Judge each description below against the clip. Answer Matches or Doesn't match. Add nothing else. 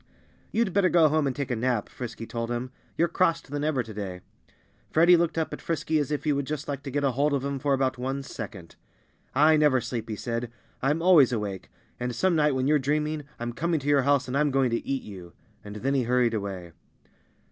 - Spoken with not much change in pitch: Doesn't match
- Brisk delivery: Matches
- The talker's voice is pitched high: Doesn't match